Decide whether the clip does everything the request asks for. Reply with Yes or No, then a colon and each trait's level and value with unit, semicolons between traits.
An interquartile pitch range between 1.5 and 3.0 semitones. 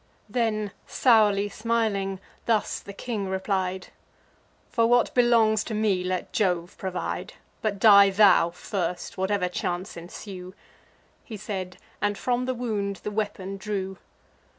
Yes: narrow, 2.5 semitones